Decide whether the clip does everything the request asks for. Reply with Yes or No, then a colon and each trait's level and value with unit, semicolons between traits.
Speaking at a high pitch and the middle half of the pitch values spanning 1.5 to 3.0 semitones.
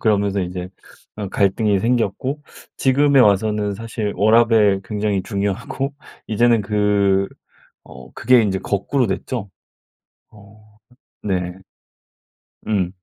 No: low, 105 Hz; narrow, 2.6 semitones